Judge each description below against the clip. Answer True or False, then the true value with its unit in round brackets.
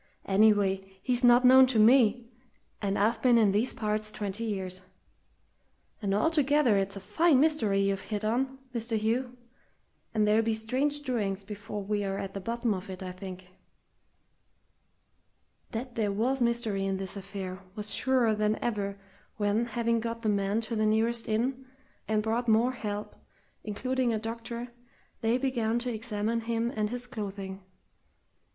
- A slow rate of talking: False (155 wpm)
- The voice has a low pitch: False (220 Hz)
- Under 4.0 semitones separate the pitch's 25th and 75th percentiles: True (2.9 semitones)